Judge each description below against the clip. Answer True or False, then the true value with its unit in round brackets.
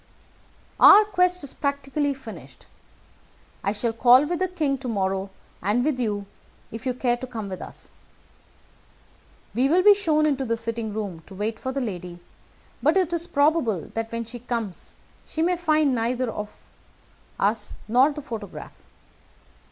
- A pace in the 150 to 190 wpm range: True (160 wpm)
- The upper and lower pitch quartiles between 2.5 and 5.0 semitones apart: False (5.4 semitones)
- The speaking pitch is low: False (245 Hz)